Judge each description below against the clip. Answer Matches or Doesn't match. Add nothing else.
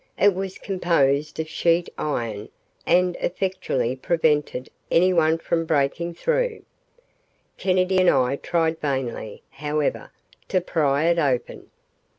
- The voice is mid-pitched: Matches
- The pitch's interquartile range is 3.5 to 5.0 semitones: Matches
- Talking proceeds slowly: Matches